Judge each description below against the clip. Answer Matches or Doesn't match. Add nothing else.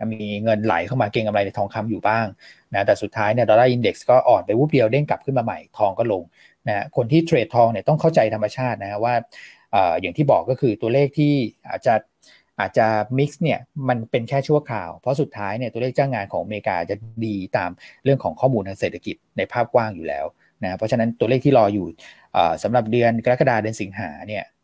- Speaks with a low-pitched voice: Matches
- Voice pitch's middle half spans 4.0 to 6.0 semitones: Doesn't match